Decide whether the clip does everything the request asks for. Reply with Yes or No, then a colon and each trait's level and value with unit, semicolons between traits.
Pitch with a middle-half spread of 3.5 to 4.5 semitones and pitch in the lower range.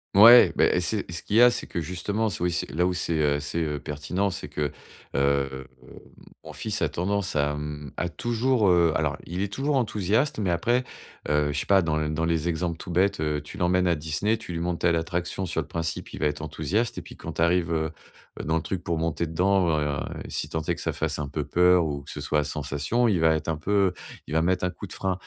Yes: average, 4.0 semitones; very low, 85 Hz